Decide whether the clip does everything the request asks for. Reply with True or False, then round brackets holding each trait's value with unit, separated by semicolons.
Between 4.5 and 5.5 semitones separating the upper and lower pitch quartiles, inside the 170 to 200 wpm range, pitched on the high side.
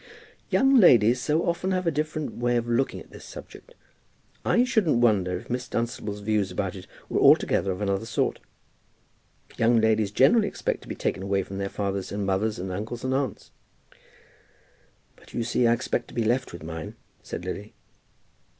False (4.9 semitones; 180 wpm; 115 Hz)